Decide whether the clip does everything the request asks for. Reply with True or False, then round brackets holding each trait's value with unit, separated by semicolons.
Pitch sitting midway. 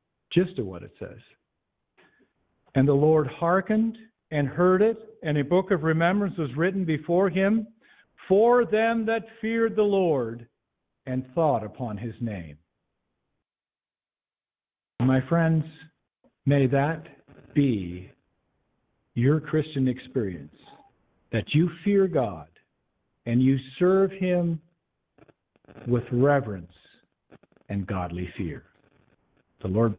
True (155 Hz)